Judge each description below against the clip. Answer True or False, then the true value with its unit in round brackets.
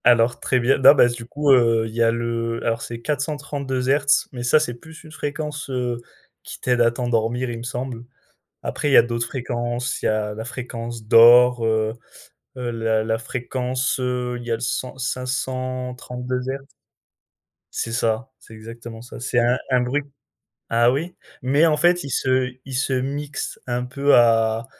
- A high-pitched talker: False (125 Hz)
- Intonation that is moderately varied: False (2.1 semitones)